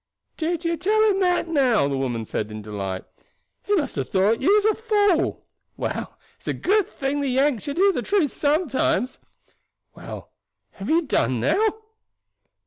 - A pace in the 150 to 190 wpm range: Yes, average, 170 wpm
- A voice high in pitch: Yes, very high, 290 Hz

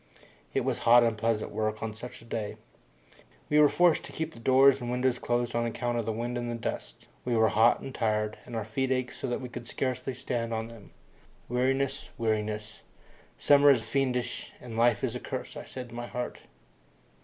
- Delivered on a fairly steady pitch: Yes, narrow, 2.3 semitones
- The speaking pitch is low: Yes, low, 120 Hz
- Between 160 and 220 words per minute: Yes, average, 200 wpm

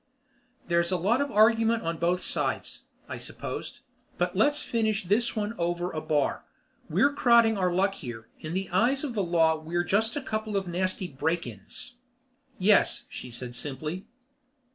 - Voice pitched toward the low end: No, medium, 185 Hz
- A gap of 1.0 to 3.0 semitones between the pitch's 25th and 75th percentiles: No, average, 5.0 semitones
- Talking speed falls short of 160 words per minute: No, average, 165 wpm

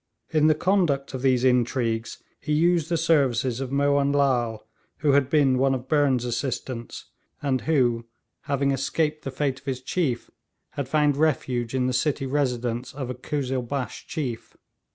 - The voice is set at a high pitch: No, low, 135 Hz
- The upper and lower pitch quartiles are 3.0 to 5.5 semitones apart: No, narrow, 2.6 semitones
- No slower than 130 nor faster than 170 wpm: Yes, average, 160 wpm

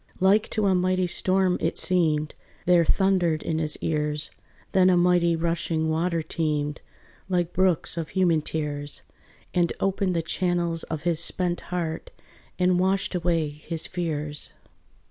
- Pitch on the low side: No, medium, 170 Hz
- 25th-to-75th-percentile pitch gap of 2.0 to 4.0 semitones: Yes, narrow, 2.4 semitones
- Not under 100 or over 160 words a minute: Yes, average, 145 wpm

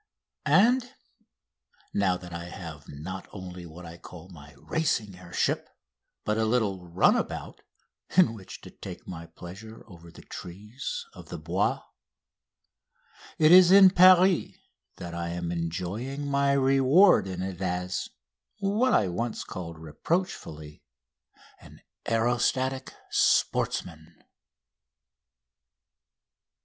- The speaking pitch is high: No, very low, 95 Hz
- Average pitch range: No, wide, 8.3 semitones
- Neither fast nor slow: No, slow, 115 wpm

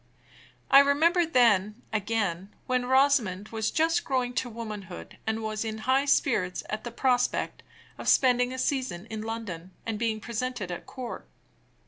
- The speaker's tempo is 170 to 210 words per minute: No, average, 150 wpm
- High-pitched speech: Yes, high, 230 Hz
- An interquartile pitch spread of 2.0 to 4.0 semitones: Yes, average, 3.5 semitones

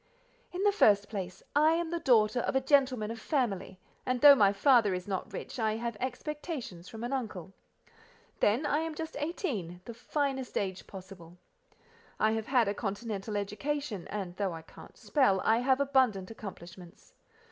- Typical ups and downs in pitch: No, wide, 5.8 semitones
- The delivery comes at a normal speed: Yes, average, 170 wpm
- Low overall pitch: No, high, 225 Hz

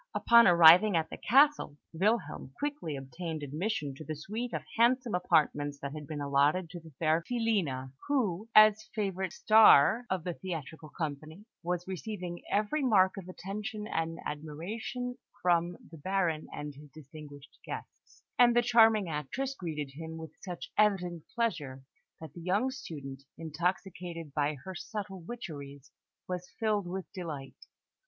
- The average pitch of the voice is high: No, medium, 175 Hz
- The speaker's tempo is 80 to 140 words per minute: No, average, 150 wpm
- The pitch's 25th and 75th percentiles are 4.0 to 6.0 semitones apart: Yes, wide, 5.6 semitones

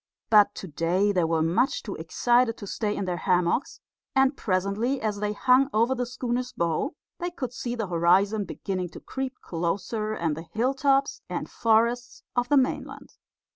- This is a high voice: Yes, high, 215 Hz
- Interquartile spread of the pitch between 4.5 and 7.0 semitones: Yes, wide, 5.5 semitones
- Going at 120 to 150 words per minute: No, average, 175 wpm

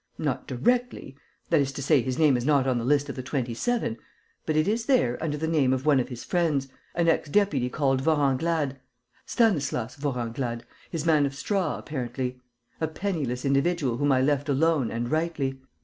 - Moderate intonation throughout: Yes, average, 3.7 semitones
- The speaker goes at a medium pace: Yes, average, 190 wpm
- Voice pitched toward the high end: No, medium, 140 Hz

